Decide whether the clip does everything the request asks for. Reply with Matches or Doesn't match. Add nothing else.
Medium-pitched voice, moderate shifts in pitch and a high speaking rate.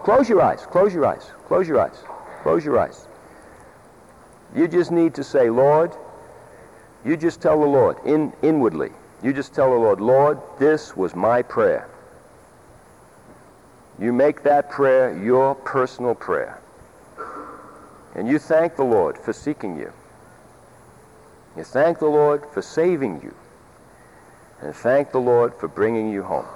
Doesn't match